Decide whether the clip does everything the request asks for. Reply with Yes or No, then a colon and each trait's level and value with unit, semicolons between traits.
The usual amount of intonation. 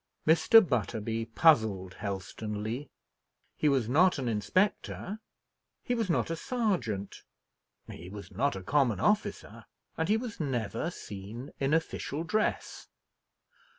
No: wide, 8.1 semitones